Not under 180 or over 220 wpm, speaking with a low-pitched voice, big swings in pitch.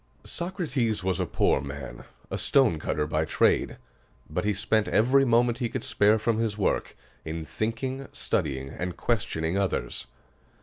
No: average, 145 wpm; low, 105 Hz; wide, 6.8 semitones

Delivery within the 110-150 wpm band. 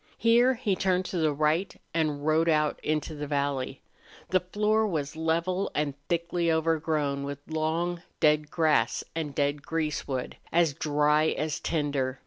Yes: average, 145 wpm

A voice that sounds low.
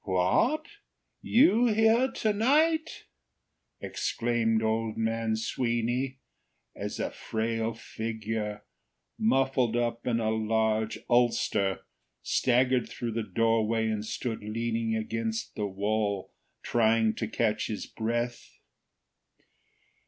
Yes: low, 115 Hz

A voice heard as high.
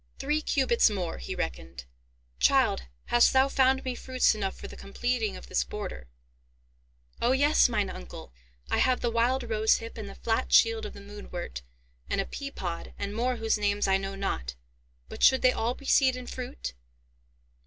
Yes: high, 225 Hz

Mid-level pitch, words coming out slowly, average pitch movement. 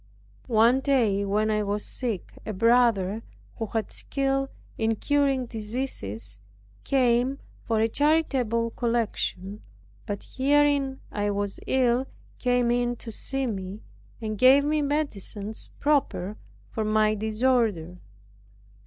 No: high, 230 Hz; slow, 120 wpm; average, 4.0 semitones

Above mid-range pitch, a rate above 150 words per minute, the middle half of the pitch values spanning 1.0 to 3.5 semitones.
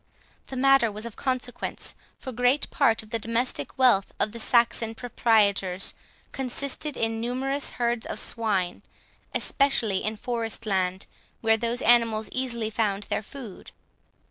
No: high, 230 Hz; average, 140 wpm; narrow, 2.6 semitones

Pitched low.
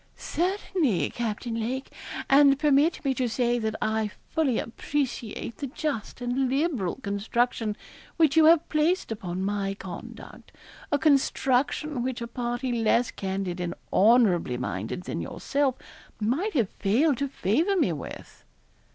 No: high, 245 Hz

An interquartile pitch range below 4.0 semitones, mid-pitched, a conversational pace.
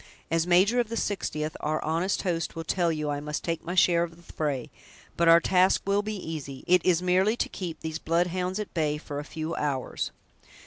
No: average, 2.9 semitones; medium, 170 Hz; fast, 220 wpm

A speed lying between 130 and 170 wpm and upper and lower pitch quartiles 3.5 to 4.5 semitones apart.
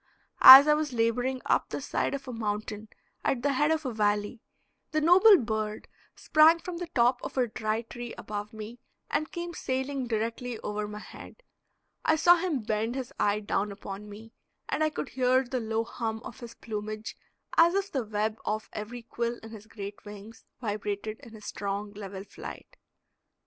No: average, 185 wpm; average, 3.9 semitones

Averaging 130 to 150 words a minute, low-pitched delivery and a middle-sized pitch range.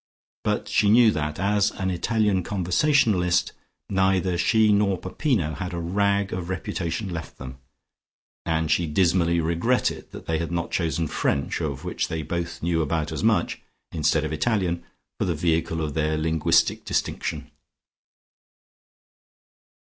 Yes: average, 140 wpm; very low, 85 Hz; average, 3.4 semitones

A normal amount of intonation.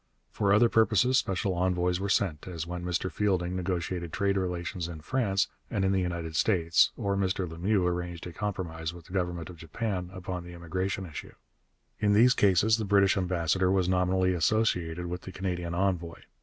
No: narrow, 2.1 semitones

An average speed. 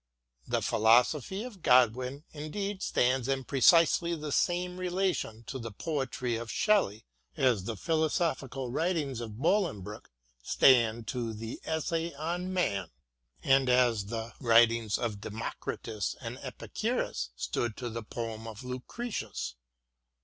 No: slow, 130 wpm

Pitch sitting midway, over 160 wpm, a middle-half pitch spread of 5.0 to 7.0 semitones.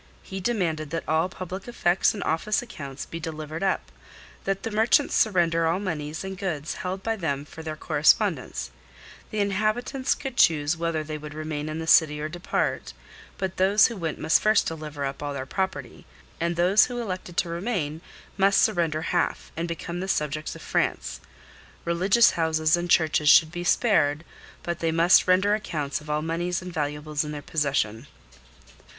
No: medium, 170 Hz; average, 175 wpm; average, 3.7 semitones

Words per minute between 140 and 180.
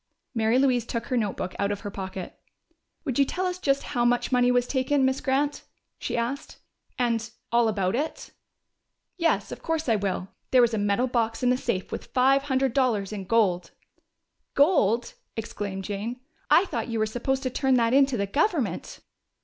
No: average, 190 wpm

